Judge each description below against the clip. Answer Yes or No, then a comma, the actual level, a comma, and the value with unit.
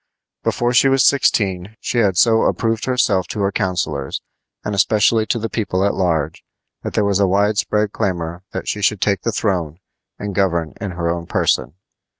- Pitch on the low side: Yes, low, 100 Hz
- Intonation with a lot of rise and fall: No, average, 3.4 semitones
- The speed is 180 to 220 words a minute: Yes, average, 185 wpm